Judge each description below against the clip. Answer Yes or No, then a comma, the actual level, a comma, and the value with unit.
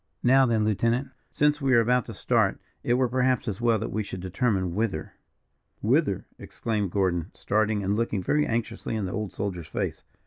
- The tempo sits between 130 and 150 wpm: No, average, 185 wpm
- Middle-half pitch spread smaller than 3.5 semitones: No, average, 3.8 semitones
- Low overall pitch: Yes, low, 110 Hz